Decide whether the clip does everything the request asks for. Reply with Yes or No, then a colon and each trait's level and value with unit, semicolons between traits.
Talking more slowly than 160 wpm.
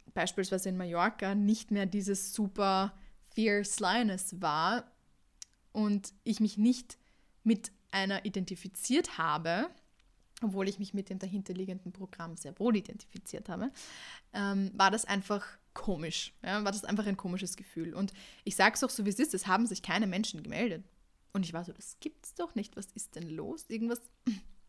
No: average, 170 wpm